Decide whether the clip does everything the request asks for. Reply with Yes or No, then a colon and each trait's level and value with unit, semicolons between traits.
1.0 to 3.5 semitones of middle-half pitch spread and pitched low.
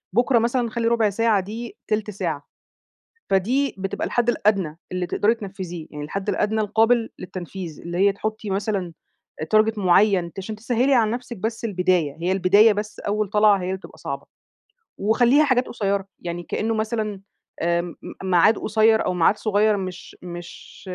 No: average, 3.2 semitones; high, 205 Hz